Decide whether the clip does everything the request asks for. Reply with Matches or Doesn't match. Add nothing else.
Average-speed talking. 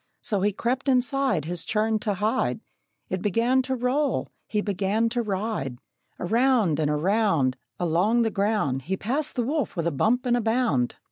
Matches